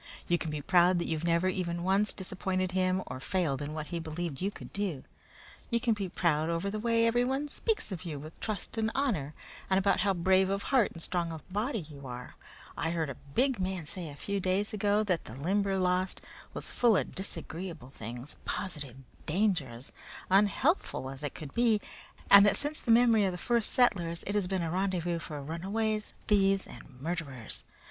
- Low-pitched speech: No, medium, 185 Hz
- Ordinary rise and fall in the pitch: Yes, average, 4.3 semitones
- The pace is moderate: Yes, average, 195 wpm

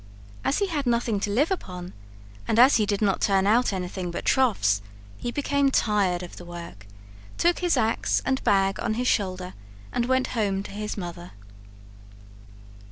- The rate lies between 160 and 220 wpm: Yes, average, 170 wpm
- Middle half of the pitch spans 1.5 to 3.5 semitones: No, average, 5.3 semitones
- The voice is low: No, high, 205 Hz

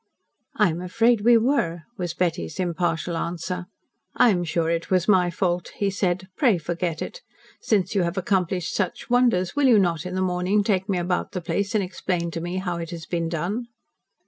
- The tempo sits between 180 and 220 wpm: Yes, average, 200 wpm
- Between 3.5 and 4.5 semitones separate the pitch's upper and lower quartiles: No, average, 2.8 semitones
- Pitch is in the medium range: Yes, medium, 180 Hz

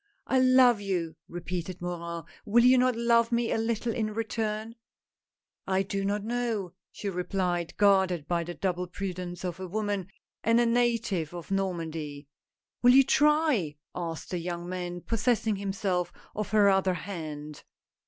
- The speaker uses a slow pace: No, average, 165 wpm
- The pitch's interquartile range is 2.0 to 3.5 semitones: No, average, 4.5 semitones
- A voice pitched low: No, high, 195 Hz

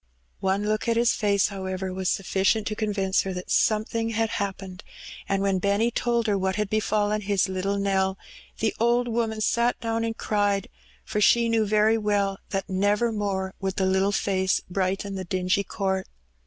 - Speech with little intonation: Yes, narrow, 2.2 semitones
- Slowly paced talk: No, average, 180 wpm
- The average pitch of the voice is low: No, high, 200 Hz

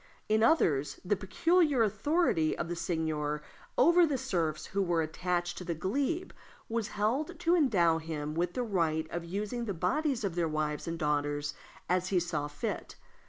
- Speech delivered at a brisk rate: No, average, 170 wpm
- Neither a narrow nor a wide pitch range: No, wide, 6.4 semitones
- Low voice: No, medium, 180 Hz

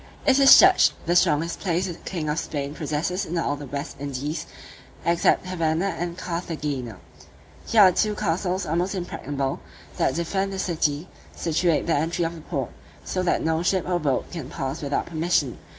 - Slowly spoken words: No, average, 180 wpm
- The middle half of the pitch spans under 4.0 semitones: Yes, average, 3.5 semitones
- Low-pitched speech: No, medium, 165 Hz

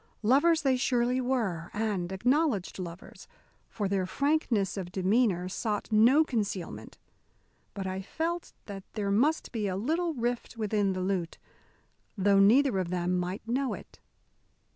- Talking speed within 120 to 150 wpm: Yes, average, 140 wpm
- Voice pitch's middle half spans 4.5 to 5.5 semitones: Yes, average, 5.1 semitones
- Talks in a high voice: Yes, high, 210 Hz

